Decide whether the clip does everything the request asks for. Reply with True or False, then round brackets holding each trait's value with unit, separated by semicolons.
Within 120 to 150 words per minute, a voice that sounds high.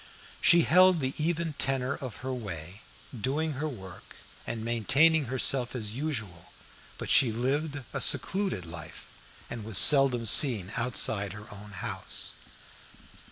False (135 wpm; 125 Hz)